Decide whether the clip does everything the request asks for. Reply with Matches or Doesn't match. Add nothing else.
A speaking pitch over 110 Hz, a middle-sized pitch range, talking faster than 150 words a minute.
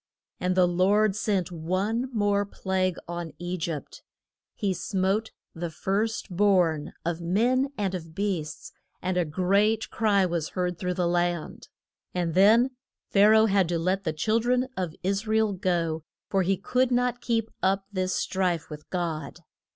Matches